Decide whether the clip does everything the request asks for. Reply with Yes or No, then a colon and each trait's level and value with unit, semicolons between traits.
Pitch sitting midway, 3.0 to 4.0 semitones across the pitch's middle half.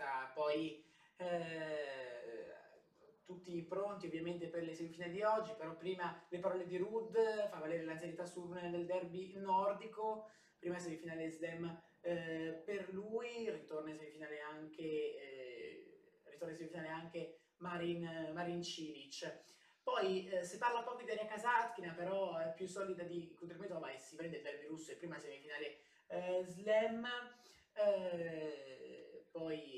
Yes: medium, 175 Hz; average, 3.7 semitones